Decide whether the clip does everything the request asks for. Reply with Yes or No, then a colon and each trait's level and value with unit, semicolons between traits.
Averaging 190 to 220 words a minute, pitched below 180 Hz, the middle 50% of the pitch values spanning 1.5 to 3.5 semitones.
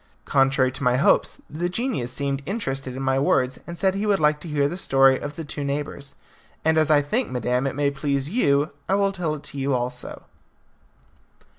Yes: fast, 205 wpm; medium, 140 Hz; average, 3.1 semitones